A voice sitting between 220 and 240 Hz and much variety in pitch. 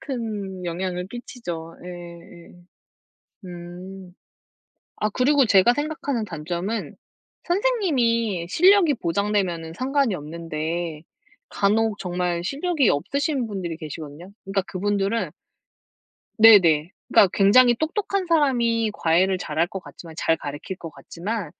No: high, 195 Hz; wide, 5.9 semitones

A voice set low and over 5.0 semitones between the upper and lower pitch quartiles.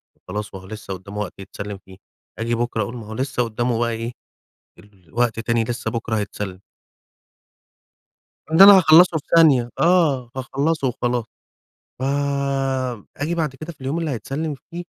Yes: low, 120 Hz; wide, 5.4 semitones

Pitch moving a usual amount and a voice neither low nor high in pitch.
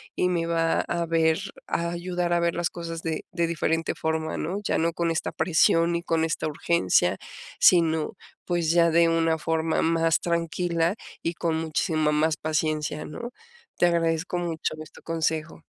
No: narrow, 1.2 semitones; medium, 165 Hz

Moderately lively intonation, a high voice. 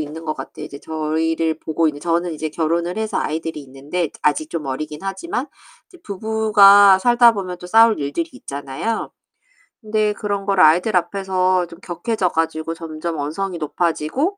No: average, 4.4 semitones; medium, 170 Hz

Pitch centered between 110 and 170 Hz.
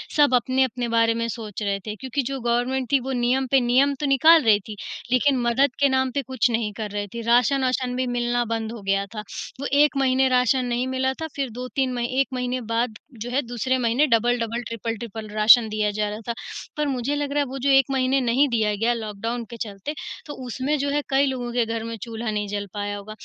No: high, 245 Hz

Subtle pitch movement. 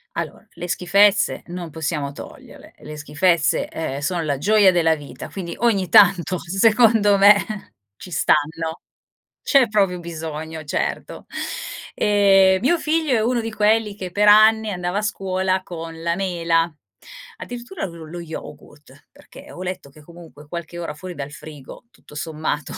No: average, 4.3 semitones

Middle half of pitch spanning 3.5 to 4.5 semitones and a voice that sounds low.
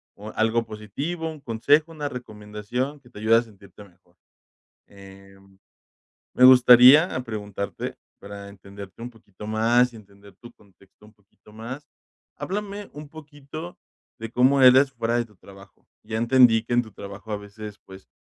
Yes: average, 4.2 semitones; low, 115 Hz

